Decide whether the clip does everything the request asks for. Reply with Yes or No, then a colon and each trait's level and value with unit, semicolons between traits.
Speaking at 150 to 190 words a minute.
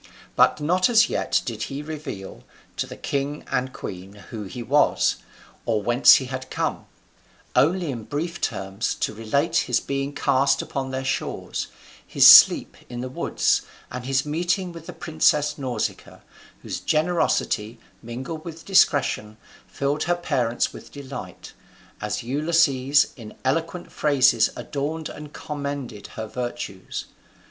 No: average, 140 wpm